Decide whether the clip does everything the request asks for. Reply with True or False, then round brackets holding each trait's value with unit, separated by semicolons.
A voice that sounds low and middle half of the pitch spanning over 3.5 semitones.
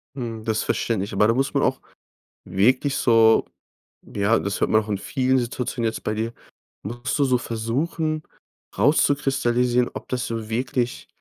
False (120 Hz; 2.5 semitones)